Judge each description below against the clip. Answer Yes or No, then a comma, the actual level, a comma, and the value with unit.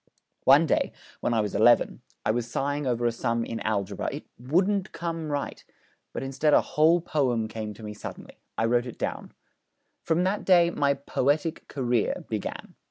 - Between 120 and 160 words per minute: No, average, 175 wpm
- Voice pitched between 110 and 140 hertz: Yes, low, 135 Hz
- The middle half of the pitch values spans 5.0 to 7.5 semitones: Yes, wide, 5.5 semitones